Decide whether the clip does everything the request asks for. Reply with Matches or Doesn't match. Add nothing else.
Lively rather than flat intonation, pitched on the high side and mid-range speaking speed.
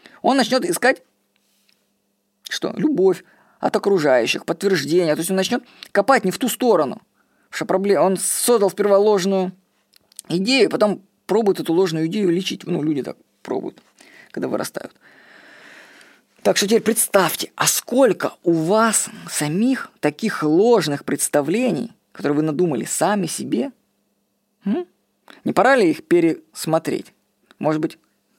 Matches